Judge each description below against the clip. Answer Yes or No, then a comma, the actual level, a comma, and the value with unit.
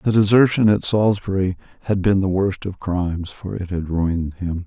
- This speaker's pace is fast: No, average, 195 wpm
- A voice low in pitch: Yes, very low, 95 Hz